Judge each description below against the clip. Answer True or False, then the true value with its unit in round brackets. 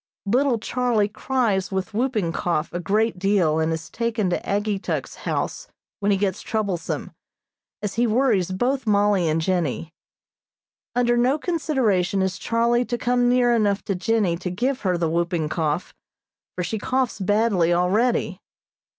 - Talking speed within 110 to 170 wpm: True (150 wpm)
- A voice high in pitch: True (205 Hz)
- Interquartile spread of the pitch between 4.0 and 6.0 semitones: True (4.9 semitones)